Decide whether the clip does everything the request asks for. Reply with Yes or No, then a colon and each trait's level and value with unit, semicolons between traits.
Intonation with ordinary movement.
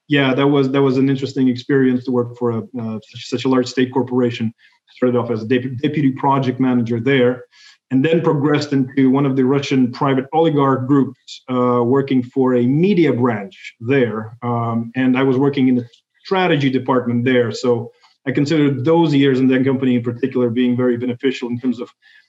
No: narrow, 1.9 semitones